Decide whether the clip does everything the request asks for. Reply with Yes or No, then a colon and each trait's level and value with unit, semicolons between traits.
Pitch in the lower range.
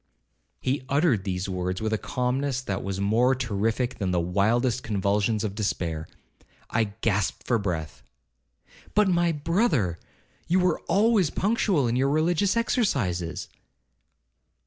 Yes: low, 115 Hz